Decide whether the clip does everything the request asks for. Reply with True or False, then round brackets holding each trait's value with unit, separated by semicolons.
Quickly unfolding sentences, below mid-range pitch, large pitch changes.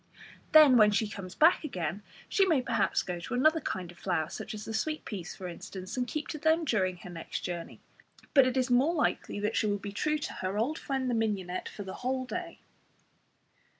False (220 wpm; 225 Hz; 7.7 semitones)